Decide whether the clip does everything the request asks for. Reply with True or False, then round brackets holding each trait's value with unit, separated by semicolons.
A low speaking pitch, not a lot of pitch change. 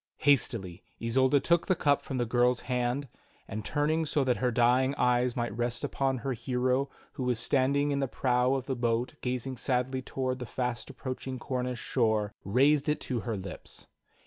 True (125 Hz; 2.0 semitones)